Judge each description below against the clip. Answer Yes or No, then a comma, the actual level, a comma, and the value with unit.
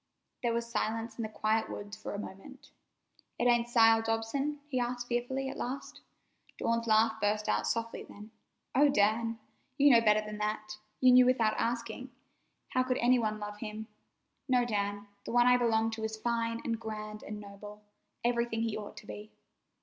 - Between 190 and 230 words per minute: No, average, 180 wpm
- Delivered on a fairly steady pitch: Yes, narrow, 2.2 semitones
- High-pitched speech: Yes, high, 225 Hz